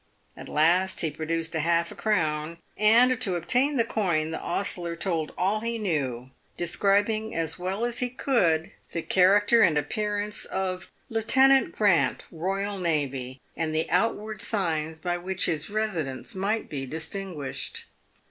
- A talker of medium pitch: Yes, medium, 180 Hz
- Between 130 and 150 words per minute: Yes, average, 140 wpm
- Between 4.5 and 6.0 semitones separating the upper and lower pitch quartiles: Yes, average, 4.9 semitones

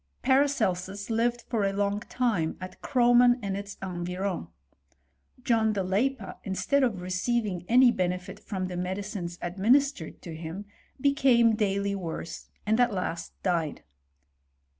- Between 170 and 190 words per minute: No, slow, 135 wpm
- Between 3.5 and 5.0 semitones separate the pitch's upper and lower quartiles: Yes, average, 4.6 semitones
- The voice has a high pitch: Yes, high, 200 Hz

